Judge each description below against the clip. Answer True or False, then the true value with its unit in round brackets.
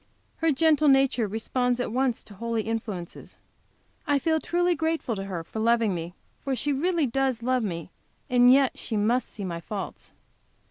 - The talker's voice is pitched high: True (245 Hz)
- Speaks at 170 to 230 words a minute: True (175 wpm)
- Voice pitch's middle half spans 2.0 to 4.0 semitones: False (4.4 semitones)